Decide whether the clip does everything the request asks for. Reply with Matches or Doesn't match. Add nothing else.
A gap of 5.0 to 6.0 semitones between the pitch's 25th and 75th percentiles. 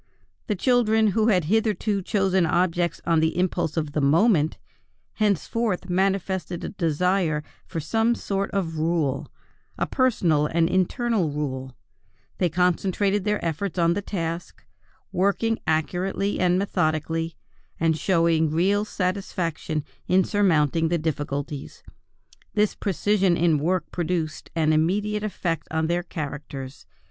Doesn't match